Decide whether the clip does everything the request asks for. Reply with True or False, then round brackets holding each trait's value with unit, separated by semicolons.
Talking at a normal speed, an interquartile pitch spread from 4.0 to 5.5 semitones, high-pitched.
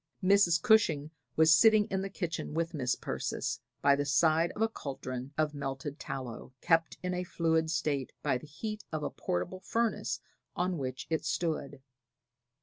False (165 wpm; 4.3 semitones; 160 Hz)